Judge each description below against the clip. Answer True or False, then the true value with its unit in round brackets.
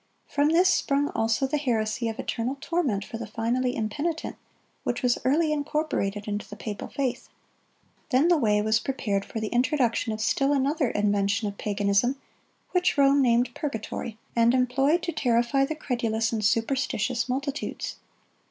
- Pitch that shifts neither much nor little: True (4.3 semitones)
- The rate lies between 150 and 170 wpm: True (155 wpm)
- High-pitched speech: True (245 Hz)